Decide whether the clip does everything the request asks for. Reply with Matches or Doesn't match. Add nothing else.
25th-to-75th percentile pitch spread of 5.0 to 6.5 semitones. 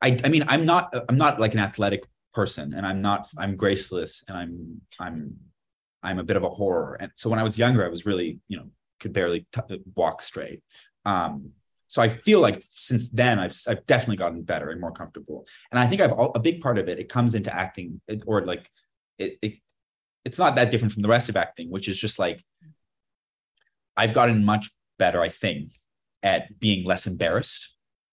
Doesn't match